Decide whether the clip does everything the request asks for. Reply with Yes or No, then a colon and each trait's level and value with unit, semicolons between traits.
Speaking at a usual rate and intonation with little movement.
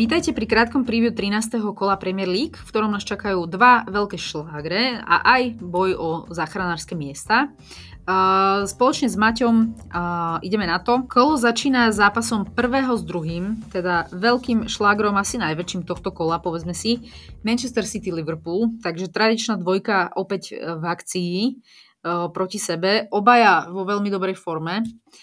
No: average, 145 wpm; average, 4.3 semitones